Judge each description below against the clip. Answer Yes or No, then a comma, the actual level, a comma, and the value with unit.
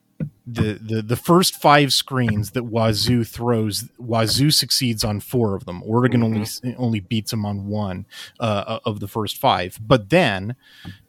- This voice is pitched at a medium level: No, low, 115 Hz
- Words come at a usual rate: Yes, average, 155 wpm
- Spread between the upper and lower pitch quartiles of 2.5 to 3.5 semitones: Yes, average, 2.8 semitones